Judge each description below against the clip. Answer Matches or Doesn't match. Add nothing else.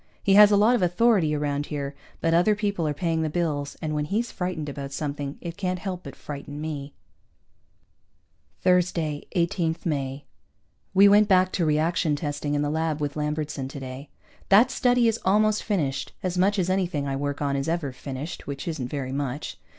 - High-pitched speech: Doesn't match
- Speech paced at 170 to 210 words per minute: Matches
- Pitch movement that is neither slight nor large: Matches